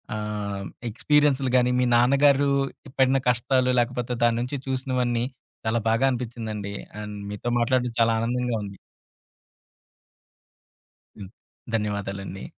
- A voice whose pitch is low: Yes, low, 120 Hz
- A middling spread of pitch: Yes, average, 3.2 semitones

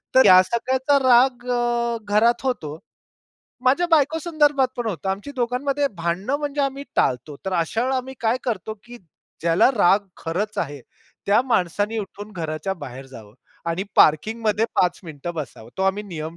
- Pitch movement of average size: No, wide, 7.0 semitones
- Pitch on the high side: Yes, high, 215 Hz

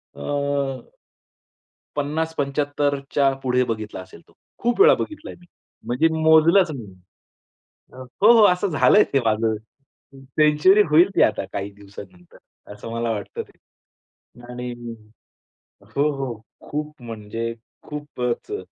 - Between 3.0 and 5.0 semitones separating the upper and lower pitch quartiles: No, wide, 5.4 semitones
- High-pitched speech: No, medium, 140 Hz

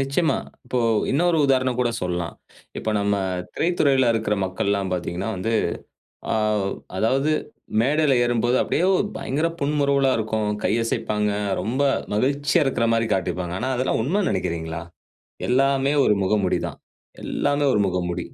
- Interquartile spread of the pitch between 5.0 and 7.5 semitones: Yes, average, 5.3 semitones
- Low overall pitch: Yes, low, 120 Hz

